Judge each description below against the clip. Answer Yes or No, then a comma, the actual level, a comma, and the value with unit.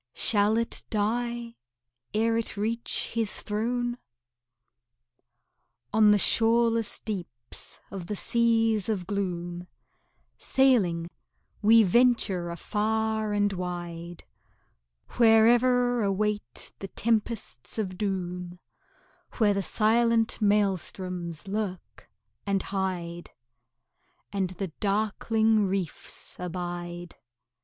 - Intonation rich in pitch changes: No, average, 3.8 semitones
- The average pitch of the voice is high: Yes, high, 205 Hz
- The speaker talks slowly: Yes, slow, 90 wpm